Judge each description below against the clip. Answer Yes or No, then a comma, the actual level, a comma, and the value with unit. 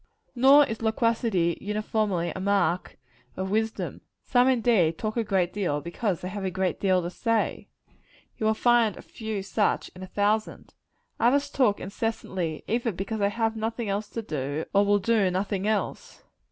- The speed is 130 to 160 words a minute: No, average, 170 wpm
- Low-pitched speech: No, high, 205 Hz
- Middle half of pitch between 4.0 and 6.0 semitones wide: No, average, 3.2 semitones